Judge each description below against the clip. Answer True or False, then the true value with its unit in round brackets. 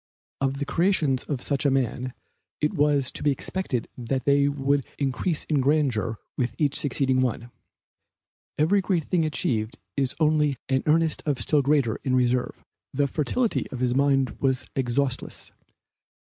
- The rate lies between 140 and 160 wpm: True (155 wpm)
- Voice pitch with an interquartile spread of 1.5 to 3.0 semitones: True (2.6 semitones)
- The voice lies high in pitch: False (140 Hz)